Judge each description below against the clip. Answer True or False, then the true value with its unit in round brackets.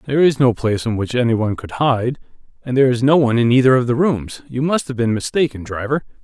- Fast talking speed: True (230 wpm)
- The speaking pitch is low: True (125 Hz)